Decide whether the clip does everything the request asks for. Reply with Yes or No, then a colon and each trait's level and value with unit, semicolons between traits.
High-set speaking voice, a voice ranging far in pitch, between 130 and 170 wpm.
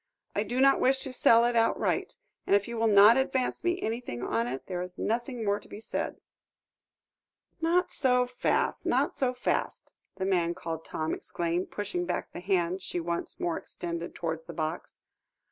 No: high, 200 Hz; wide, 6.2 semitones; average, 180 wpm